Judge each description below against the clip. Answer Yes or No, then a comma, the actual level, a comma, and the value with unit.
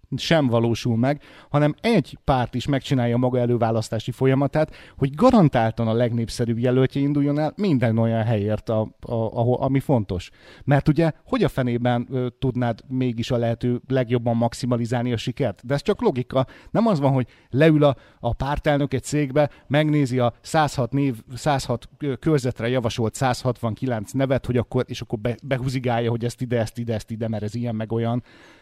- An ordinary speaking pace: No, fast, 160 wpm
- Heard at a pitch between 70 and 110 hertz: No, low, 125 Hz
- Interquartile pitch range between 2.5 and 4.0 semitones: Yes, average, 3.1 semitones